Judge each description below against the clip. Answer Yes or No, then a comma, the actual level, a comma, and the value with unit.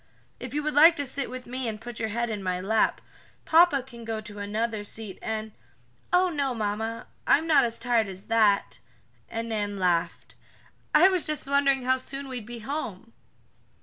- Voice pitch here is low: No, high, 230 Hz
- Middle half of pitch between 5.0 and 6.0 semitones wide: No, average, 4.5 semitones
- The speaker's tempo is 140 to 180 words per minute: No, average, 190 wpm